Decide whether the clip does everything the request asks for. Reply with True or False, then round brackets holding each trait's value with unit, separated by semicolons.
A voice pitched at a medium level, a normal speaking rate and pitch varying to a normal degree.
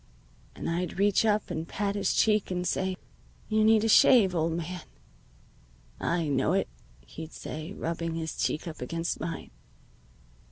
True (175 Hz; 155 wpm; 3.8 semitones)